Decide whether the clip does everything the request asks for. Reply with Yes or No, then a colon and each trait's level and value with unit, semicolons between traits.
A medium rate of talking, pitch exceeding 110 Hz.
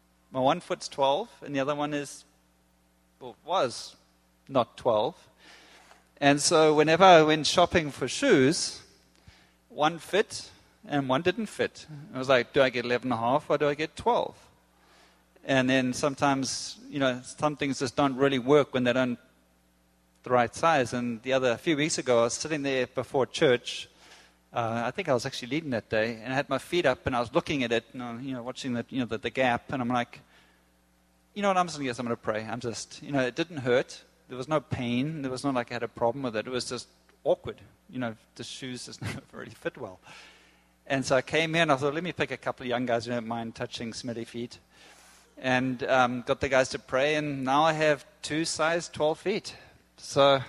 No: fast, 220 wpm; low, 130 Hz